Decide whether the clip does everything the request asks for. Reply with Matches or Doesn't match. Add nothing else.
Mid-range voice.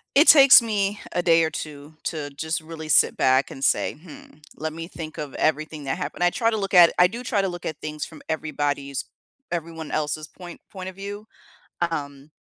Matches